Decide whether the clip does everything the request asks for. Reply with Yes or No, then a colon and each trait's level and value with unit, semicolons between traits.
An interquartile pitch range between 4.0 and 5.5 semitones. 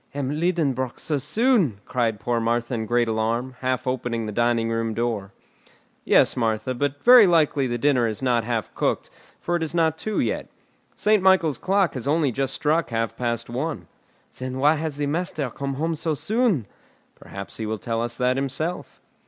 Yes: average, 5.2 semitones